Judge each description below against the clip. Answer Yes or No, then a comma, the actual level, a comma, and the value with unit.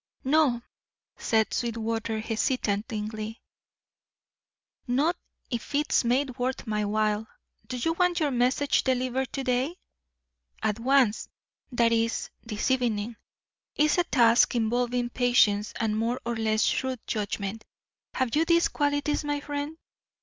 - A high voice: Yes, high, 245 Hz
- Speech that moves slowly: Yes, slow, 125 wpm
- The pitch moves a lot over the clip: No, average, 3.6 semitones